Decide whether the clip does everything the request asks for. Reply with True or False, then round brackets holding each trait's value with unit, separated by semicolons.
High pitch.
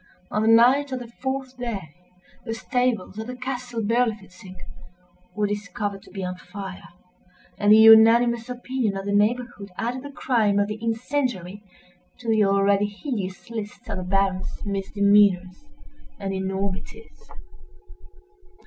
True (215 Hz)